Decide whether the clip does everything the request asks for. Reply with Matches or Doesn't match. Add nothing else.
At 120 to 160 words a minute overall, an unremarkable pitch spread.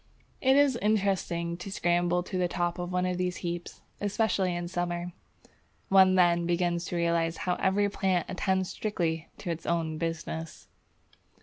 Doesn't match